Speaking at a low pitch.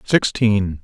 Yes: low, 105 Hz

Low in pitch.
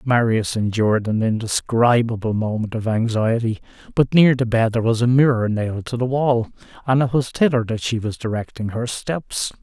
Yes: low, 115 Hz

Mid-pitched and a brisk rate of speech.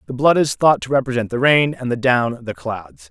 No: low, 120 Hz; fast, 250 wpm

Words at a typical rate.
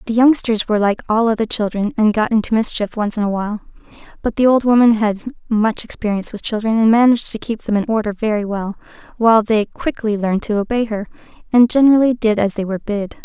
No: fast, 210 wpm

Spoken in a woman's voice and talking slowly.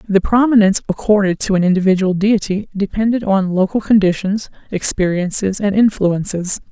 Yes: female; slow, 125 wpm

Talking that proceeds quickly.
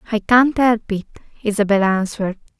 No: average, 140 wpm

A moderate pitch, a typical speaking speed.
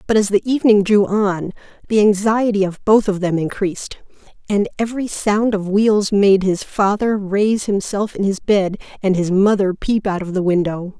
No: high, 200 Hz; average, 185 wpm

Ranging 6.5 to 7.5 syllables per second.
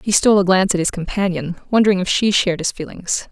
Yes: 6.8 syllables/s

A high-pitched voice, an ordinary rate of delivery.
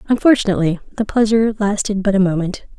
Yes: high, 205 Hz; average, 150 wpm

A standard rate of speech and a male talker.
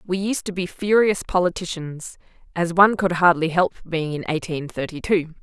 No: average, 175 wpm; female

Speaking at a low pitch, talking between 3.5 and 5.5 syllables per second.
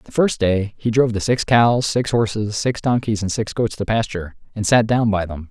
Yes: low, 110 Hz; 5.1 syllables/s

